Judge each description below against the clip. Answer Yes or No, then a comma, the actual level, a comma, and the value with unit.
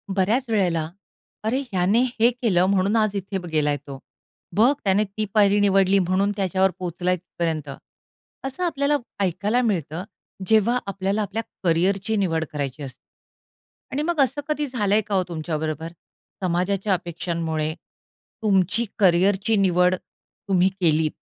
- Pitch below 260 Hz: Yes, high, 190 Hz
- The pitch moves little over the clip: No, average, 3.8 semitones